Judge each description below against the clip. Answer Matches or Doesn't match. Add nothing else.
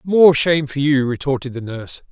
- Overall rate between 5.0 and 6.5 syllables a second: Matches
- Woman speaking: Doesn't match